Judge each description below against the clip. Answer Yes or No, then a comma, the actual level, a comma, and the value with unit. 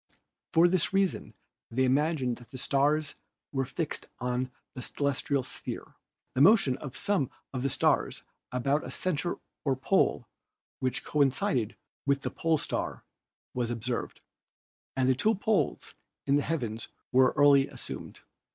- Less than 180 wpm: Yes, average, 140 wpm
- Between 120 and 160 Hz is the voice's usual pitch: Yes, medium, 140 Hz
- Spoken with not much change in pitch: No, average, 3.5 semitones